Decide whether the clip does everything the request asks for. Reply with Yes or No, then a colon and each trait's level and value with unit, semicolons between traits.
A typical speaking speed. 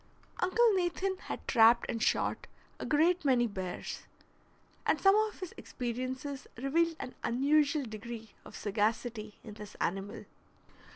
No: slow, 130 wpm